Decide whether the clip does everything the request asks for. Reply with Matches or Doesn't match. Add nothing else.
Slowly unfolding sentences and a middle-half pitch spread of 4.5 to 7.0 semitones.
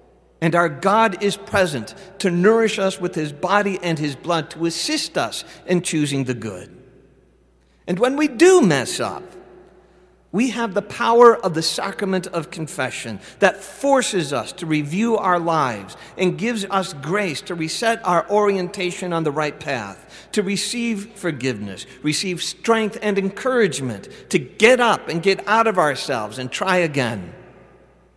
Doesn't match